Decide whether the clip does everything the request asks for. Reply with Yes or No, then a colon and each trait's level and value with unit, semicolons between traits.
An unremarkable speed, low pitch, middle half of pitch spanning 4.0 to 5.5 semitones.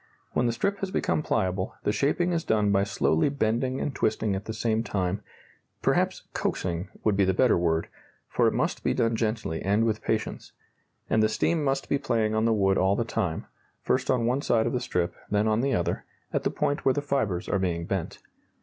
No: fast, 215 wpm; low, 110 Hz; average, 4.5 semitones